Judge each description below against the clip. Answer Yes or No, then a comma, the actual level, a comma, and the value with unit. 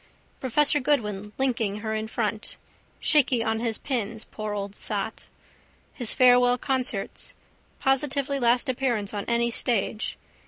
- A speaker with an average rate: No, slow, 125 wpm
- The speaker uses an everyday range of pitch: Yes, average, 3.3 semitones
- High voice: Yes, high, 235 Hz